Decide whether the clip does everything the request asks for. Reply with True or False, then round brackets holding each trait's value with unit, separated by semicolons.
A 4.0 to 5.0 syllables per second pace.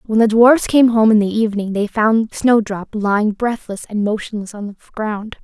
True (4.9 syllables/s)